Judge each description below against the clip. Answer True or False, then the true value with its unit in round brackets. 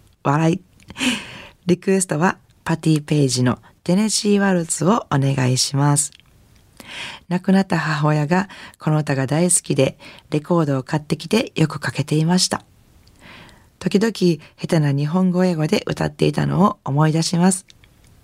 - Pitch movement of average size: True (4.0 semitones)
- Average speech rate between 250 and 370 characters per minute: True (290 characters per minute)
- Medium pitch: True (165 Hz)